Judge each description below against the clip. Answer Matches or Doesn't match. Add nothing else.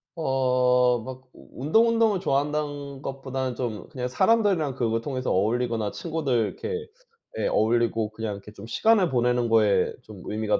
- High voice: Doesn't match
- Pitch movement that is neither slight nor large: Matches